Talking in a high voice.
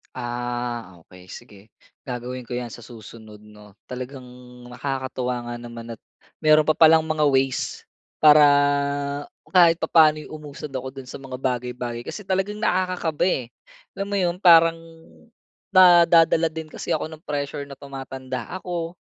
No: low, 135 Hz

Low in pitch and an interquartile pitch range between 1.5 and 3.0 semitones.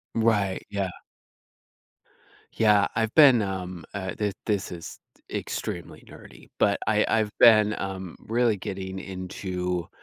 Yes: low, 100 Hz; narrow, 2.5 semitones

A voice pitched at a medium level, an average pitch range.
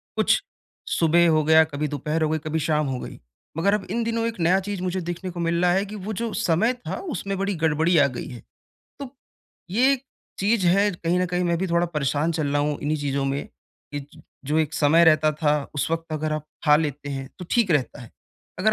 Yes: medium, 165 Hz; average, 4.1 semitones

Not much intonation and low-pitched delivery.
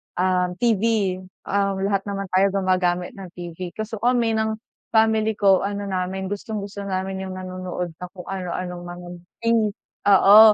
No: narrow, 2.0 semitones; high, 195 Hz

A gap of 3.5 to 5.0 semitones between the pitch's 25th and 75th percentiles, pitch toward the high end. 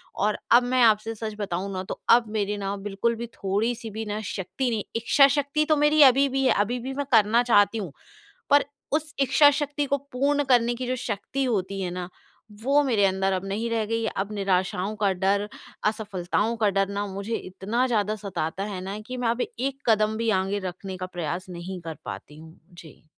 Yes: average, 4.2 semitones; high, 215 Hz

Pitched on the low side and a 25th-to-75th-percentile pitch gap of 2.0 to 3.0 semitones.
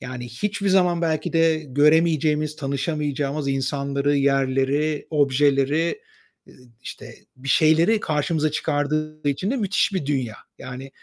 No: medium, 150 Hz; average, 2.7 semitones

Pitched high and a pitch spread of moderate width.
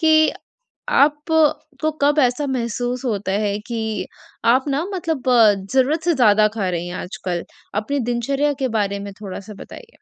No: very high, 255 Hz; wide, 5.9 semitones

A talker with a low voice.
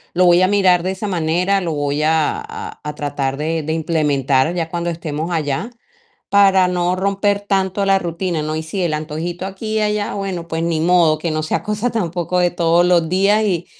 No: medium, 175 Hz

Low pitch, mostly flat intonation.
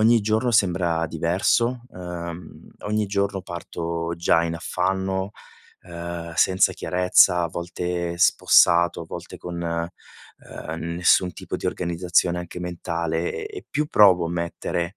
Yes: very low, 85 Hz; narrow, 2.0 semitones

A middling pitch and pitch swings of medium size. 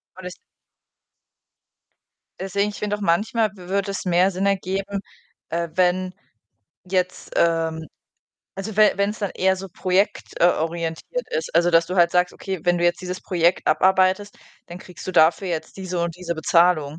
No: medium, 180 Hz; narrow, 2.2 semitones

